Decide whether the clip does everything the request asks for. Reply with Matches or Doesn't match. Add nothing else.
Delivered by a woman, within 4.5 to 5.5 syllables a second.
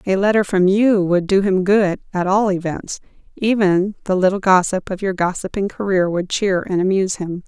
Matches